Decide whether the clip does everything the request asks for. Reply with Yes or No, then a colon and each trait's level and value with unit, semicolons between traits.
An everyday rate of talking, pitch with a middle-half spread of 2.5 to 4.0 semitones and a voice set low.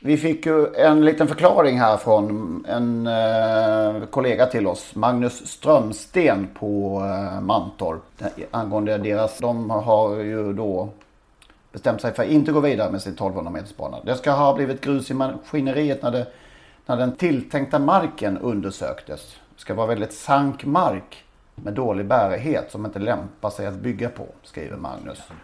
No: average, 150 wpm; average, 4.9 semitones; low, 115 Hz